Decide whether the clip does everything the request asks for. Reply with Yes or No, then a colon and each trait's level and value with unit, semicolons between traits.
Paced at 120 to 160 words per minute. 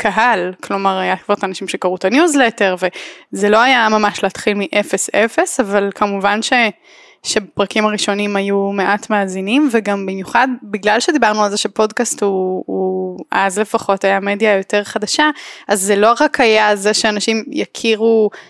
Yes: fast, 150 wpm